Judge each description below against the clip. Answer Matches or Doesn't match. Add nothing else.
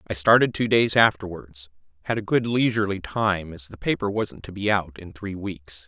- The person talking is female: Doesn't match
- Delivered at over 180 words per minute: Matches